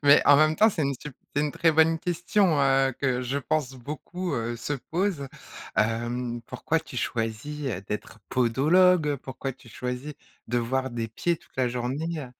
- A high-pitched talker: No, low, 135 Hz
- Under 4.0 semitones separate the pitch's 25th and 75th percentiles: No, average, 4.3 semitones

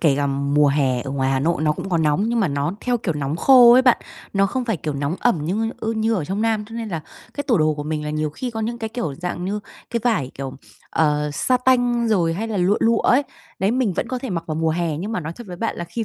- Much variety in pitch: Yes, wide, 7.1 semitones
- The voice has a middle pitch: Yes, medium, 180 Hz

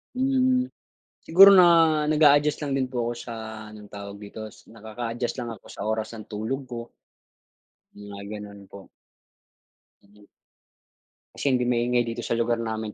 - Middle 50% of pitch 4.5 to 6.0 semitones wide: Yes, average, 4.8 semitones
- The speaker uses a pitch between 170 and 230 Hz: No, low, 115 Hz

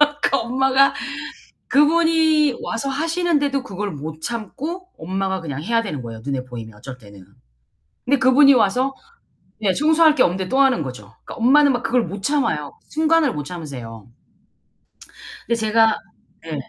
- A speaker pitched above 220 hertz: Yes, high, 230 Hz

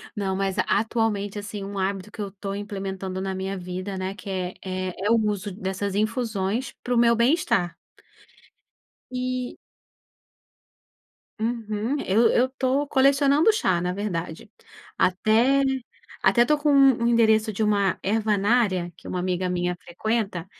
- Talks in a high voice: Yes, high, 205 Hz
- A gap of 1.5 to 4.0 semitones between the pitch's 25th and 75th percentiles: Yes, average, 3.7 semitones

